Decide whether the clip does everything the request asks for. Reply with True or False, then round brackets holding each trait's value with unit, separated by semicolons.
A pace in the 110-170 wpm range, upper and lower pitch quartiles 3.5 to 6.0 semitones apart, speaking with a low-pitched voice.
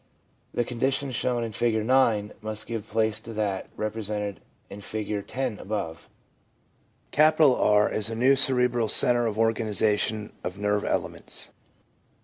False (135 wpm; 2.6 semitones; 110 Hz)